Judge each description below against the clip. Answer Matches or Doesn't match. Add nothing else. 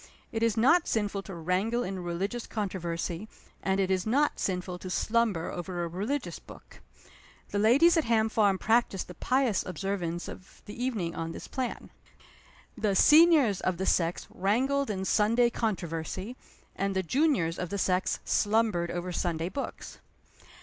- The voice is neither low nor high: Doesn't match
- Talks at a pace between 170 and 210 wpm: Doesn't match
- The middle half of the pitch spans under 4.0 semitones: Doesn't match